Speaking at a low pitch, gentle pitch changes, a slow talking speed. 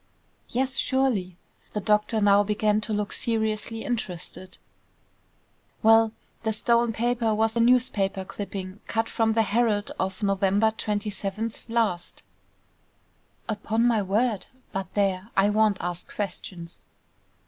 No: high, 215 Hz; narrow, 2.3 semitones; slow, 120 wpm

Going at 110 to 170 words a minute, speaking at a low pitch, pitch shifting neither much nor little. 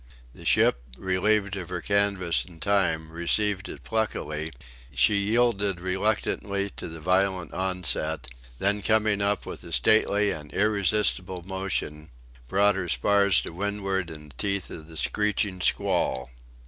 Yes: average, 140 wpm; very low, 95 Hz; average, 3.3 semitones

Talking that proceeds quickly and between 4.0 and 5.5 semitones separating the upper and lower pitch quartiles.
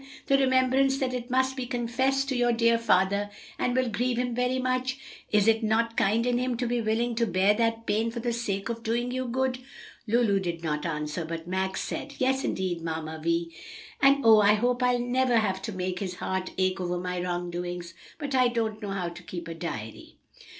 Yes: fast, 210 wpm; average, 5.2 semitones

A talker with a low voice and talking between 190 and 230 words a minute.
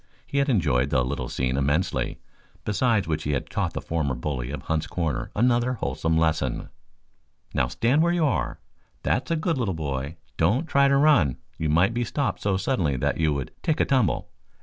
Yes: very low, 85 Hz; average, 195 wpm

